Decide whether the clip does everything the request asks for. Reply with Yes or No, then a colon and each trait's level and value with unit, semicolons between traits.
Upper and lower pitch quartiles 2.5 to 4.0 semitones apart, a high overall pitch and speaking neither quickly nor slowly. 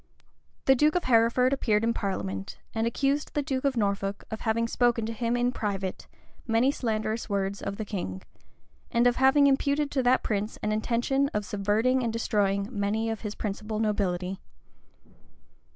Yes: average, 3.7 semitones; high, 225 Hz; average, 170 wpm